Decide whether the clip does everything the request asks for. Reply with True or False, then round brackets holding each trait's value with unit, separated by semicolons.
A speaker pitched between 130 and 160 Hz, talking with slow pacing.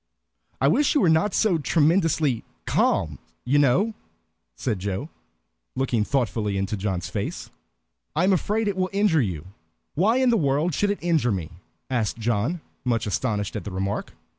False (135 Hz; 165 wpm)